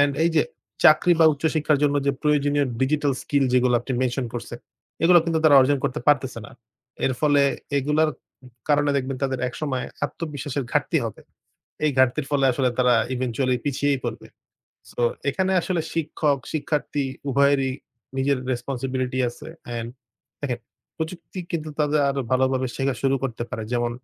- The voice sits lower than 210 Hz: Yes, medium, 140 Hz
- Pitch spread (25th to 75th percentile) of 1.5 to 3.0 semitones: Yes, narrow, 2.5 semitones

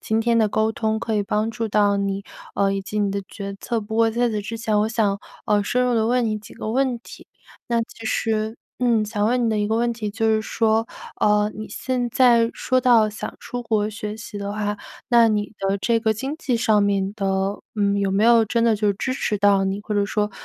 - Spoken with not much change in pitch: Yes, narrow, 1.9 semitones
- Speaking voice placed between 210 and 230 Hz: Yes, high, 220 Hz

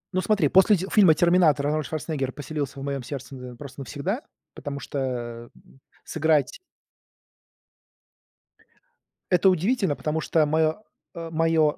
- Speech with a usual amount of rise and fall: Yes, average, 3.7 semitones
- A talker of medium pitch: Yes, medium, 155 Hz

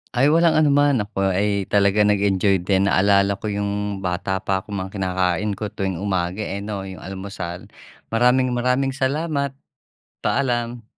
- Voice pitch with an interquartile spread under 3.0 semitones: No, average, 4.3 semitones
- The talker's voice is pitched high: No, low, 100 Hz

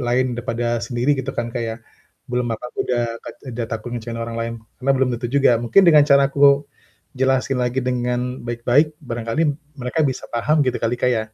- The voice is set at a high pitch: No, low, 125 Hz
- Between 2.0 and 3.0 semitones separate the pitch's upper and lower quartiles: Yes, narrow, 2.6 semitones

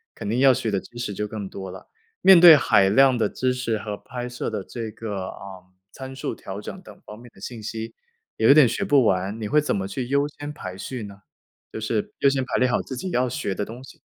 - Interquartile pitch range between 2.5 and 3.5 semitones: No, average, 4.4 semitones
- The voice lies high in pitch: No, low, 115 Hz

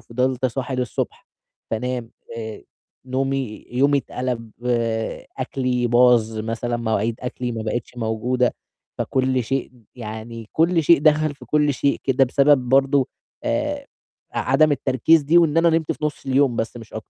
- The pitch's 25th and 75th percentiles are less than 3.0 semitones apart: No, average, 3.3 semitones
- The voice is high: No, low, 130 Hz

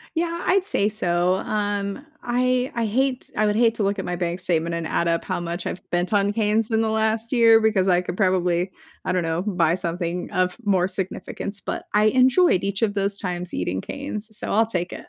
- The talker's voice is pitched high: Yes, high, 200 Hz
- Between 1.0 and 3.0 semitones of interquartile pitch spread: No, average, 3.9 semitones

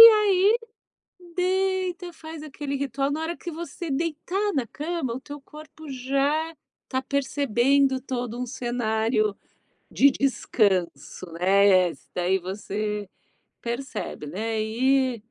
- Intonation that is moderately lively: No, wide, 6.2 semitones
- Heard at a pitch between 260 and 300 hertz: Yes, very high, 270 Hz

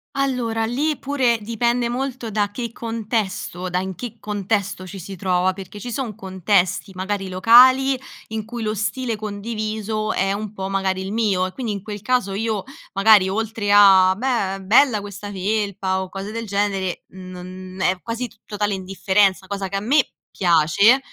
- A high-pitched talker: Yes, high, 205 Hz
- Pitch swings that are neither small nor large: Yes, average, 3.1 semitones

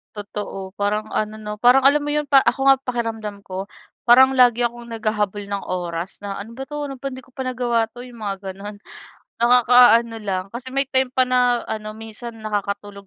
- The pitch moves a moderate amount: Yes, average, 3.6 semitones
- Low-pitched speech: No, high, 230 Hz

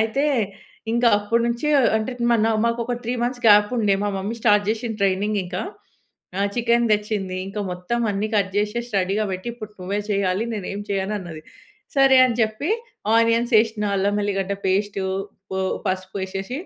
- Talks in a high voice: Yes, high, 210 Hz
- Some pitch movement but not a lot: Yes, average, 3.0 semitones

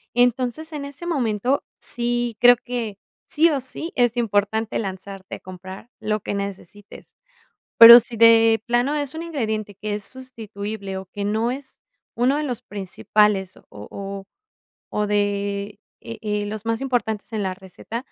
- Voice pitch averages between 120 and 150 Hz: No, high, 220 Hz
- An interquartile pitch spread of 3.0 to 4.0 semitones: Yes, average, 3.4 semitones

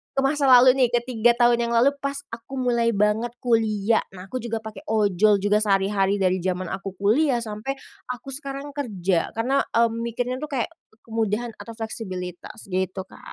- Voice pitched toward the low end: No, high, 230 Hz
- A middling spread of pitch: Yes, average, 3.5 semitones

